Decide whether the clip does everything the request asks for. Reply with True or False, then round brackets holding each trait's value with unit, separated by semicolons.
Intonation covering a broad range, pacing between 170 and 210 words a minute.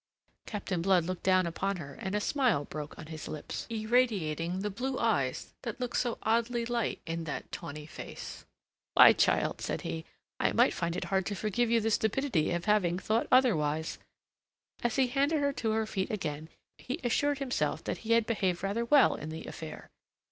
True (6.1 semitones; 190 wpm)